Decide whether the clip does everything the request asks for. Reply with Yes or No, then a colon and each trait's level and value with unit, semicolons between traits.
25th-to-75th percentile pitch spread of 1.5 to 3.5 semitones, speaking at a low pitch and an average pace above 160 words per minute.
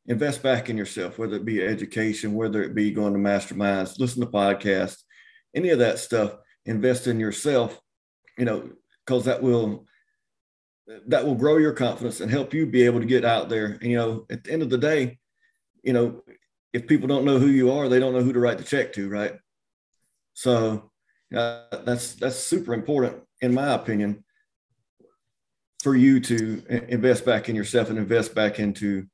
Yes: average, 3.2 semitones; low, 120 Hz; average, 185 wpm